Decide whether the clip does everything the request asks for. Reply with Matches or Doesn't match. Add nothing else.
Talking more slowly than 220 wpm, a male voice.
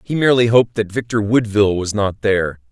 Matches